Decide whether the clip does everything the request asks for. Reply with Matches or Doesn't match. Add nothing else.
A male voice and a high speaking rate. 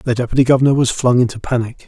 Matches